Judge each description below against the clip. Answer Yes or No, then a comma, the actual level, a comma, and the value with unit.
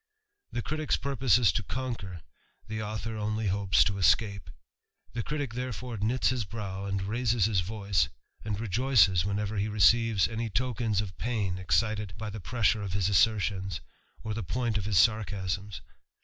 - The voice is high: No, low, 105 Hz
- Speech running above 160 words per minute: No, average, 150 wpm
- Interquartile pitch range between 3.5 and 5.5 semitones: No, average, 2.7 semitones